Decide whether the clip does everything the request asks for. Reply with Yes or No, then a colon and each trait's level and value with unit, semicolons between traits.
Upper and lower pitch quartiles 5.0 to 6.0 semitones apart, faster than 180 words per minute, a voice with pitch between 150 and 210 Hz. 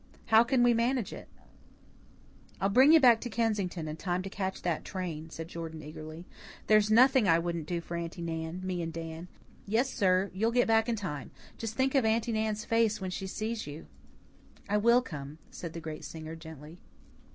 Yes: wide, 5.5 semitones; average, 195 wpm; high, 190 Hz